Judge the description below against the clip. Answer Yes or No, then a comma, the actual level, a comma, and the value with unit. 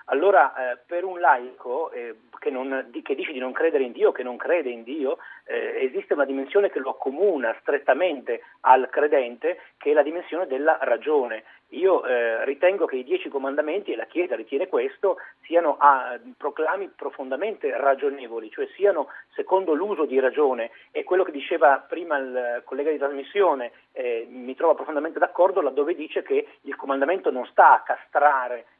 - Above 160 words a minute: Yes, fast, 170 wpm